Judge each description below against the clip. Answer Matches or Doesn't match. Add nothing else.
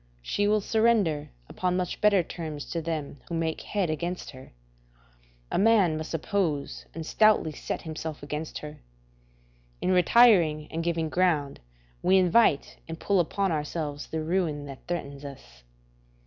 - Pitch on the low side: Doesn't match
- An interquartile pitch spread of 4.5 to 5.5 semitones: Doesn't match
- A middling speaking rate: Matches